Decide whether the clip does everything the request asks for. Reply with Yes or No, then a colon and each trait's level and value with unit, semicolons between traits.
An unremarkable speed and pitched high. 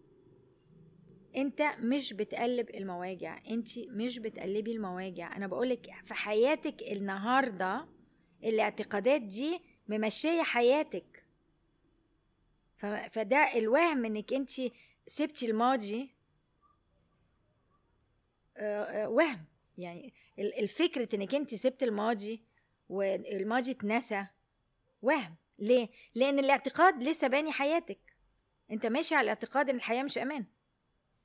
Yes: average, 90 wpm; high, 230 Hz